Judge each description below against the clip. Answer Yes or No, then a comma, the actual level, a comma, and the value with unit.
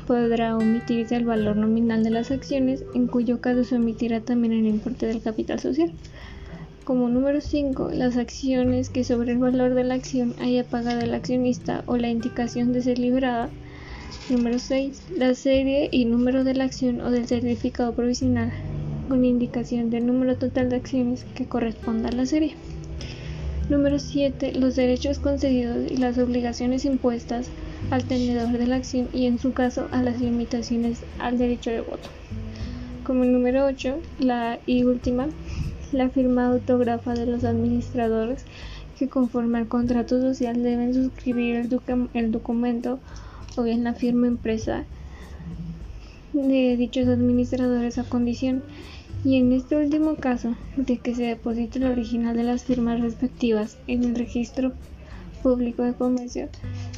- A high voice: Yes, high, 245 Hz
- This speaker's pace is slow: No, average, 155 wpm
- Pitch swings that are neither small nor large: No, narrow, 1.4 semitones